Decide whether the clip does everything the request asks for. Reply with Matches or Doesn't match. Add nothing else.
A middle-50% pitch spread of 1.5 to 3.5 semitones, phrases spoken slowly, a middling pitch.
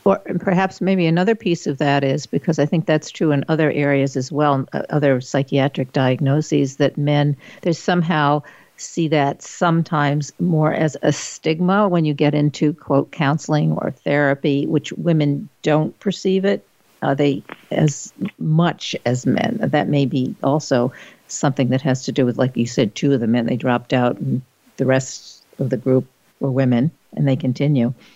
Doesn't match